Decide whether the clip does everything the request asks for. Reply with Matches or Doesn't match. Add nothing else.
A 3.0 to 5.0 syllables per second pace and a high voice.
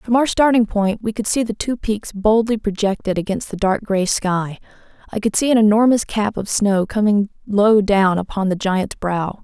Matches